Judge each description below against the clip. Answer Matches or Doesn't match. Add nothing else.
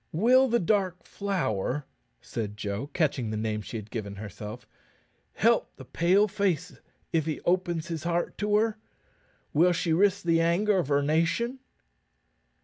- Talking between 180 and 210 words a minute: Doesn't match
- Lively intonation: Matches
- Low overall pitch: Doesn't match